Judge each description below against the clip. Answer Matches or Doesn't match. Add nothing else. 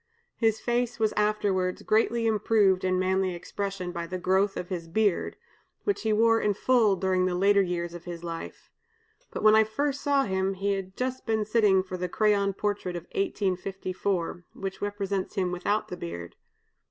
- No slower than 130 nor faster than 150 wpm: Doesn't match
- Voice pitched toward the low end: Doesn't match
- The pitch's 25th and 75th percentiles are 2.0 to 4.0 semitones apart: Matches